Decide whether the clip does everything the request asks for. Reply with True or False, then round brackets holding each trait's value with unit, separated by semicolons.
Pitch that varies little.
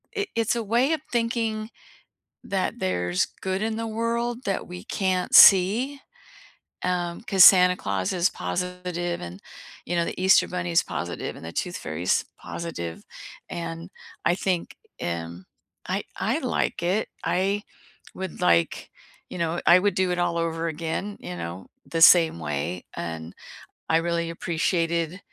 False (3.5 semitones)